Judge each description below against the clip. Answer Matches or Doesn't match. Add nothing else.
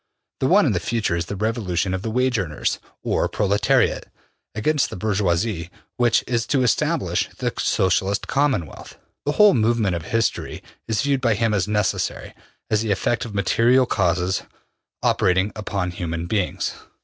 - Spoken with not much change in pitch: Doesn't match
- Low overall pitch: Matches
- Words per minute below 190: Matches